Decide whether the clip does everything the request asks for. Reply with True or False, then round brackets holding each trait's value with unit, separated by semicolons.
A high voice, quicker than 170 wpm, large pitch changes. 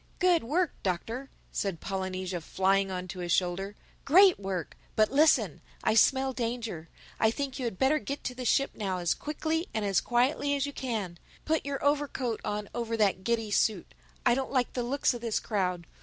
True (230 Hz; 185 wpm; 6.2 semitones)